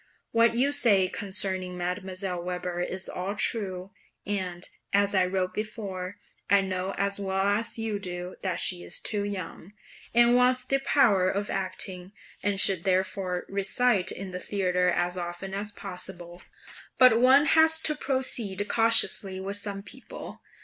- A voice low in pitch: No, high, 195 Hz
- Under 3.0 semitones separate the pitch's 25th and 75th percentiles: Yes, narrow, 2.6 semitones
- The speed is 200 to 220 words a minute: No, average, 150 wpm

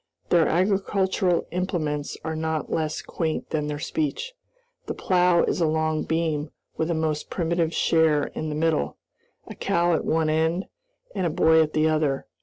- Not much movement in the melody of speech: Yes, narrow, 2.0 semitones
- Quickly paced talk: No, average, 170 wpm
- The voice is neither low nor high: Yes, medium, 160 Hz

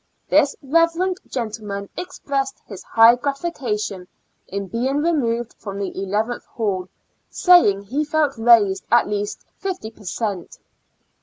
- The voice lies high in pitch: Yes, high, 230 Hz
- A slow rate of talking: Yes, slow, 125 wpm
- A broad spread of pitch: Yes, wide, 5.9 semitones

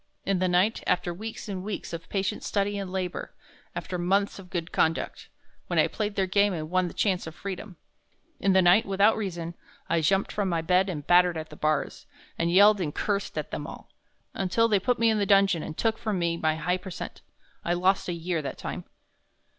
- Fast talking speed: Yes, fast, 215 wpm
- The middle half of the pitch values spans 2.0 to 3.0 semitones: Yes, narrow, 2.6 semitones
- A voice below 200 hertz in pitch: Yes, medium, 185 Hz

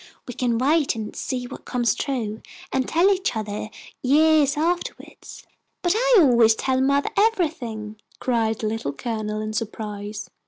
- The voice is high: Yes, high, 245 Hz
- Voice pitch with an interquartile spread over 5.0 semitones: Yes, wide, 5.5 semitones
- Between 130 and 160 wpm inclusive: Yes, average, 150 wpm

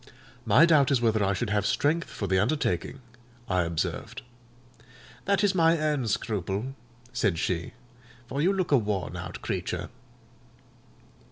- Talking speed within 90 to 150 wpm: Yes, average, 145 wpm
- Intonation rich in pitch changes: Yes, wide, 7.6 semitones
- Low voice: Yes, low, 115 Hz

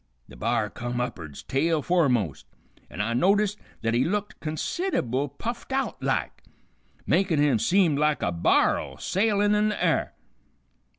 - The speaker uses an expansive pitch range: Yes, wide, 9.0 semitones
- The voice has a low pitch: No, medium, 150 Hz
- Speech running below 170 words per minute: Yes, average, 140 wpm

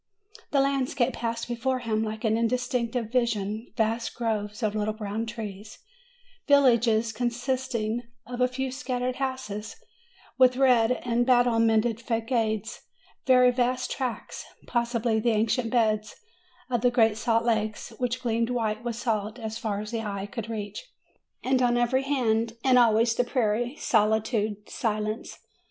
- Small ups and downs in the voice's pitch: Yes, narrow, 2.3 semitones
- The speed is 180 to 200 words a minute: No, average, 145 wpm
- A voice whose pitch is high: Yes, high, 230 Hz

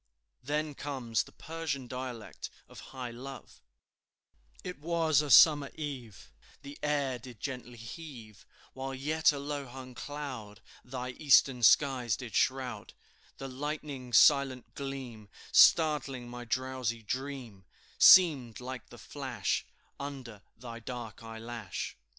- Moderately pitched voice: No, low, 130 Hz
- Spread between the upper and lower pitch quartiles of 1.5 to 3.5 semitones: Yes, average, 3.0 semitones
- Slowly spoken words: Yes, slow, 120 wpm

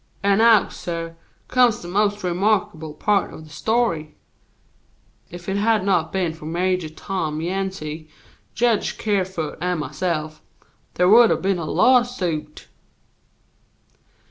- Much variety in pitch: No, average, 4.3 semitones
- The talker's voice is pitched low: No, medium, 185 Hz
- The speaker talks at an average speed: No, slow, 125 wpm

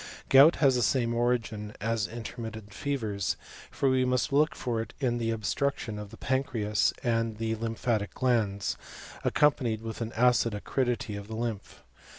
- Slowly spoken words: No, average, 160 wpm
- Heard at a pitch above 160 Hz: No, low, 115 Hz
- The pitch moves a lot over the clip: No, narrow, 2.6 semitones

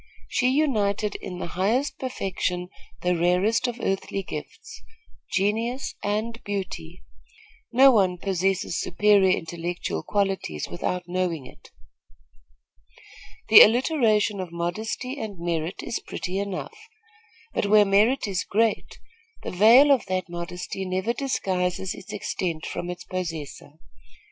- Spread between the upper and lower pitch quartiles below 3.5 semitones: No, average, 4.0 semitones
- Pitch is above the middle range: Yes, high, 195 Hz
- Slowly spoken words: Yes, slow, 120 wpm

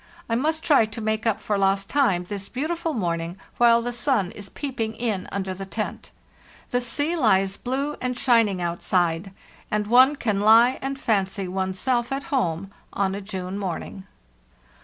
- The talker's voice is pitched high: Yes, high, 215 Hz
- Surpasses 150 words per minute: Yes, average, 170 wpm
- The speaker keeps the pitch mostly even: No, average, 4.6 semitones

